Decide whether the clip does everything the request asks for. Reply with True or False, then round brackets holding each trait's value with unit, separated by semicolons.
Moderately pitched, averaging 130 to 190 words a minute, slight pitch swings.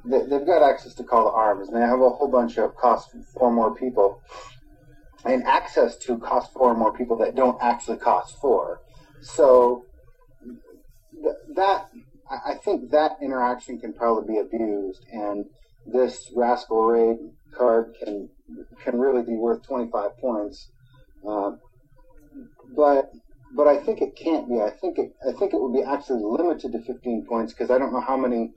False (120 Hz; 165 wpm; 2.2 semitones)